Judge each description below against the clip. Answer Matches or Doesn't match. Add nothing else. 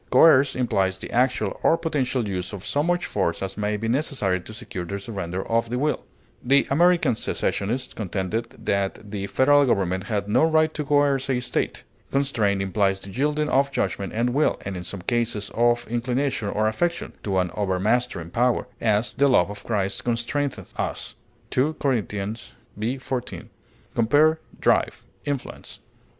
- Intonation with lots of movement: Matches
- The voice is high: Doesn't match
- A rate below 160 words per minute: Doesn't match